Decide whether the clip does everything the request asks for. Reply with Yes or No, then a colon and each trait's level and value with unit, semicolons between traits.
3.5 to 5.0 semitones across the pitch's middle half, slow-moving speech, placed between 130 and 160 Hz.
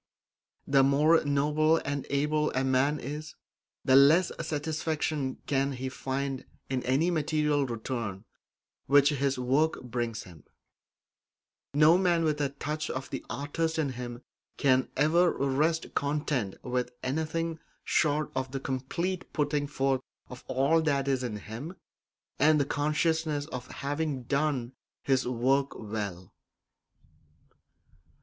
No: average, 2.8 semitones; slow, 130 wpm; medium, 140 Hz